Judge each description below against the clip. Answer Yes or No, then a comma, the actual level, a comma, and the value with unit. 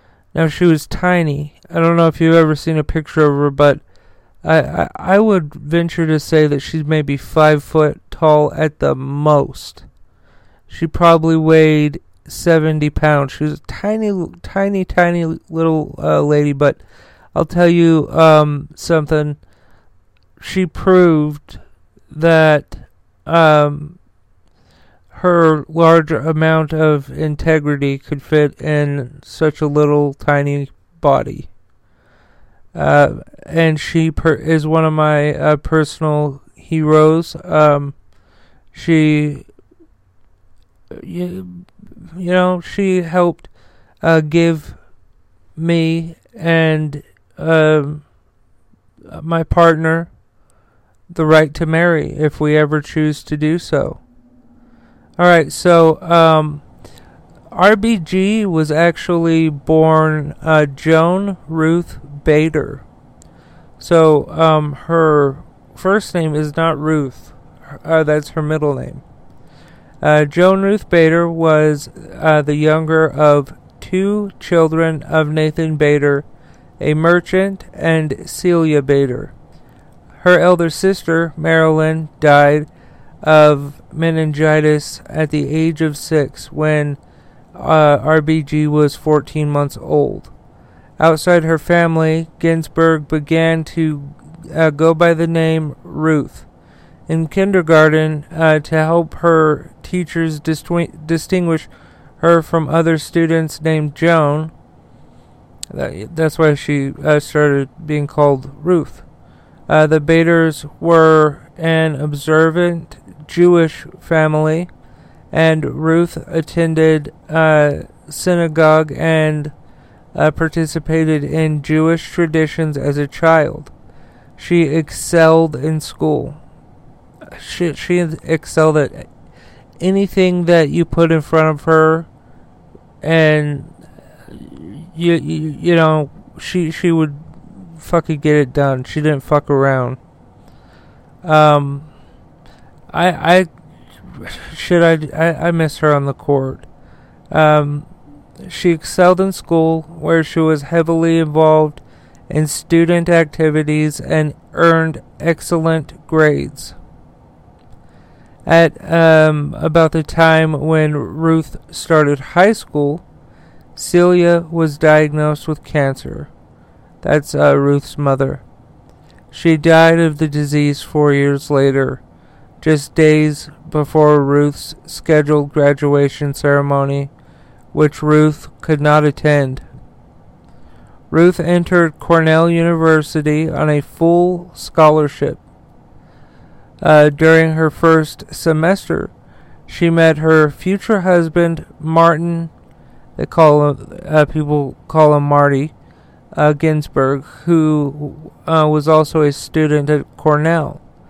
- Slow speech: Yes, slow, 110 wpm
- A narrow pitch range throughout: Yes, narrow, 1.8 semitones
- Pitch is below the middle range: No, medium, 155 Hz